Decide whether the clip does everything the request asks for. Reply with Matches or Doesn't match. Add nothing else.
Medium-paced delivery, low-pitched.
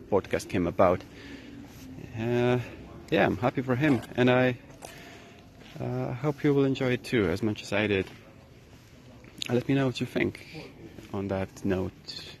Matches